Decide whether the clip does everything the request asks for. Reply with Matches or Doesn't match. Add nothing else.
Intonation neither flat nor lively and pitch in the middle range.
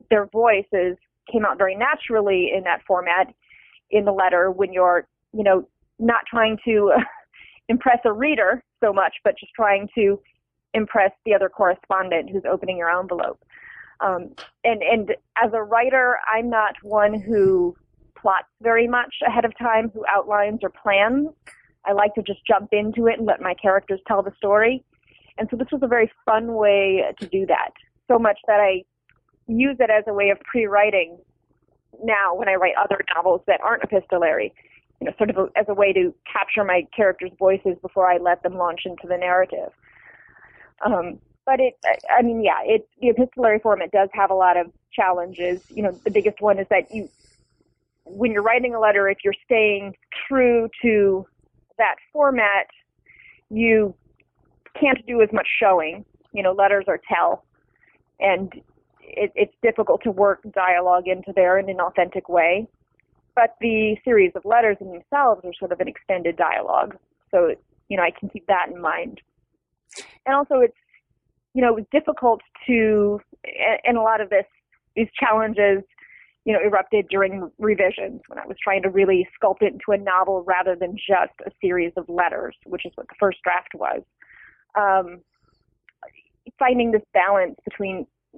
Doesn't match